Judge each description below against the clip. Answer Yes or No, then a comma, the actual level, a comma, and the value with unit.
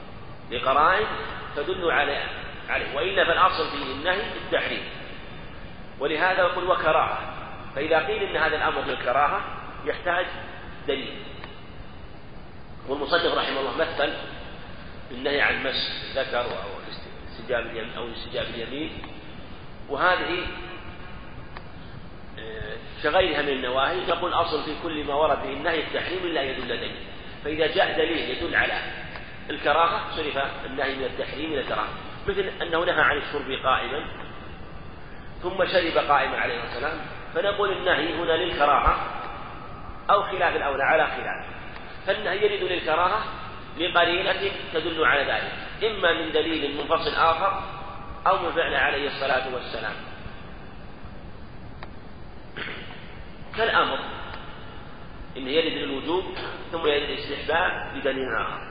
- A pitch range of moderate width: Yes, average, 3.9 semitones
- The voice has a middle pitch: Yes, medium, 180 Hz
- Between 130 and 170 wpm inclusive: No, average, 110 wpm